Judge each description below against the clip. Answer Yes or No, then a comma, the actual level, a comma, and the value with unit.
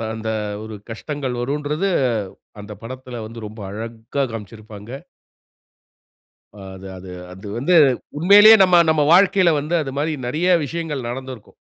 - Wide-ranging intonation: Yes, wide, 6.5 semitones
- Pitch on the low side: Yes, low, 130 Hz